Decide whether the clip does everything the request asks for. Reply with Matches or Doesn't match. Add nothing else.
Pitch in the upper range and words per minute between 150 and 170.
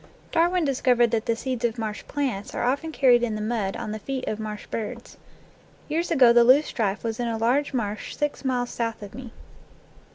Doesn't match